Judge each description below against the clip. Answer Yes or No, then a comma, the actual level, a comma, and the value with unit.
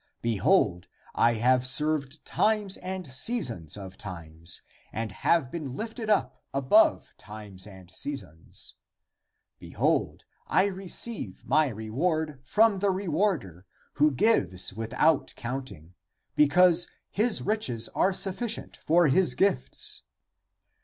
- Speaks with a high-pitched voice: No, medium, 140 Hz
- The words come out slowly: Yes, slow, 115 wpm